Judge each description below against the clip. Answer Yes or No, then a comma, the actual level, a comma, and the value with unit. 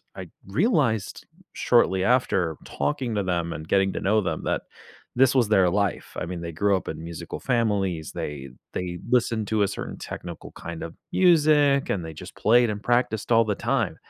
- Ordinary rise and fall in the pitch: No, wide, 5.7 semitones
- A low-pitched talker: Yes, low, 100 Hz